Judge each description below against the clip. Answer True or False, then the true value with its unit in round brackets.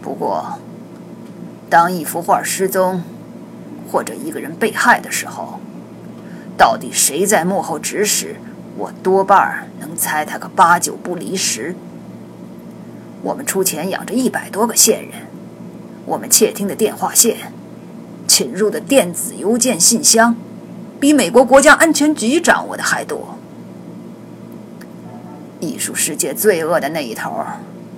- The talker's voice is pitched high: True (210 Hz)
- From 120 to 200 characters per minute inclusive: True (195 characters per minute)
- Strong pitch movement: False (4.7 semitones)